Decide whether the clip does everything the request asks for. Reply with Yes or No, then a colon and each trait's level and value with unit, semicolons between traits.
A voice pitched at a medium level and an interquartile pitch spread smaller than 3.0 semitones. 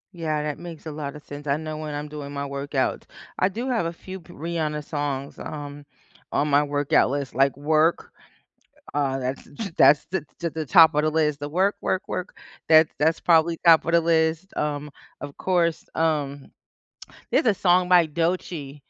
Yes: medium, 155 Hz; narrow, 2.6 semitones